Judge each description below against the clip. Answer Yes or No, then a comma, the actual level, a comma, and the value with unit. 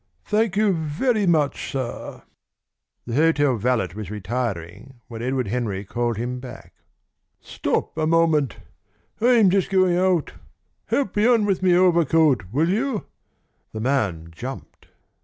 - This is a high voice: No, medium, 145 Hz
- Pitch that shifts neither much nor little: No, wide, 7.7 semitones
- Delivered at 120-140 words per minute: Yes, slow, 135 wpm